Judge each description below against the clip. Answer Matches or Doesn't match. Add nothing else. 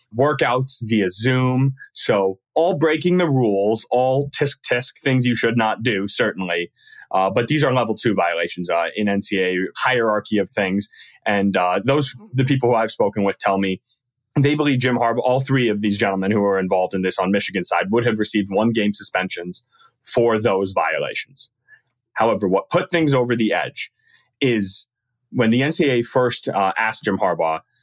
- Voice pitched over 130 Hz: Doesn't match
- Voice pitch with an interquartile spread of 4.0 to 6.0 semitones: Matches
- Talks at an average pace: Matches